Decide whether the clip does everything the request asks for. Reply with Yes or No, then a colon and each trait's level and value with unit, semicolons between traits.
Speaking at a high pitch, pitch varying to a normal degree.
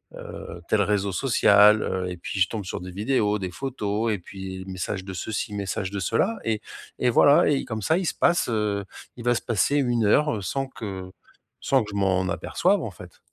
No: low, 105 Hz; average, 4.3 semitones